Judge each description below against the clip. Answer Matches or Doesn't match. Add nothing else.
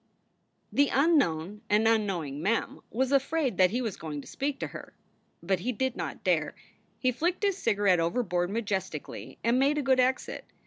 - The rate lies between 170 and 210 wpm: Matches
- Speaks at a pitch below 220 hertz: Doesn't match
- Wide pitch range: Matches